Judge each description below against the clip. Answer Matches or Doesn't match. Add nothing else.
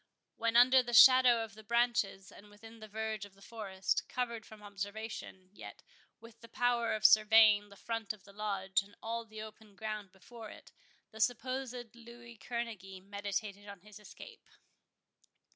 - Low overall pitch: Doesn't match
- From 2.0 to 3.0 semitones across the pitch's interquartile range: Matches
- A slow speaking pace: Doesn't match